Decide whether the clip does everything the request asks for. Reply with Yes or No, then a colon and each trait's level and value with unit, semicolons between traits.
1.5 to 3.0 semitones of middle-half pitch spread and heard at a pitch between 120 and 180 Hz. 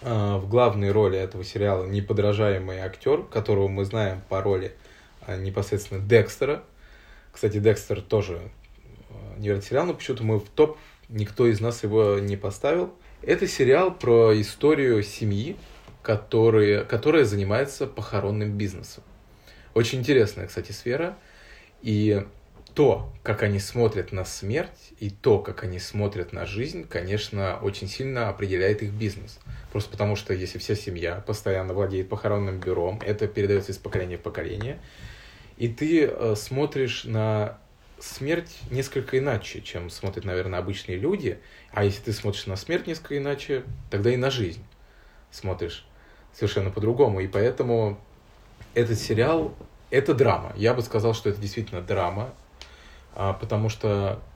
No: narrow, 2.6 semitones; low, 105 Hz